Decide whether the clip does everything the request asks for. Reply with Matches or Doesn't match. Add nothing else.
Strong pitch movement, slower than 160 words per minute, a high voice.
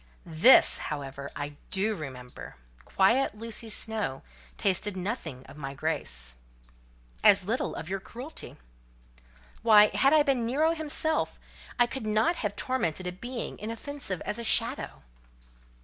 Matches